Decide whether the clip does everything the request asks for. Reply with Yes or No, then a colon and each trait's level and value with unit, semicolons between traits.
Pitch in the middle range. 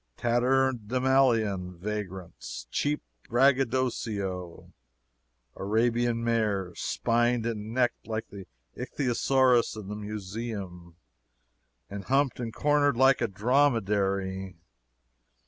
No: low, 115 Hz